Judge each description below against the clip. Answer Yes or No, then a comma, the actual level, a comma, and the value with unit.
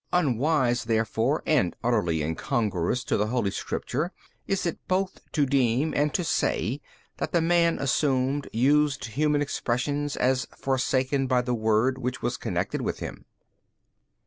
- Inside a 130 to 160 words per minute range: Yes, average, 145 wpm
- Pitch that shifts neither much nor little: Yes, average, 3.9 semitones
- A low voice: Yes, low, 130 Hz